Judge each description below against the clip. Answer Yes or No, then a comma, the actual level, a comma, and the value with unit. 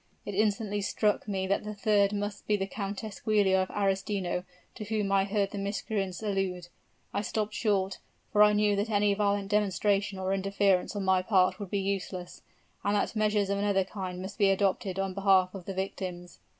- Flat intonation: Yes, narrow, 1.4 semitones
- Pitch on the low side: No, high, 200 Hz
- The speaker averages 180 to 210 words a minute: Yes, average, 190 wpm